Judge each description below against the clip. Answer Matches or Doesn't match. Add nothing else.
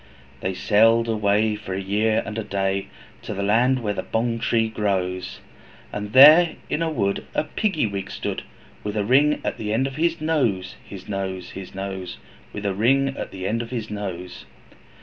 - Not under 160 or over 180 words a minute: Doesn't match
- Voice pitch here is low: Matches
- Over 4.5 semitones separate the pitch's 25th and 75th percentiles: Doesn't match